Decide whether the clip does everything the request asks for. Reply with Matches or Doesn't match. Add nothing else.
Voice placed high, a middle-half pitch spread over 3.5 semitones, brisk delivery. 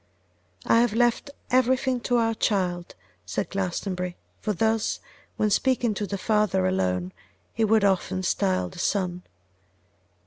Doesn't match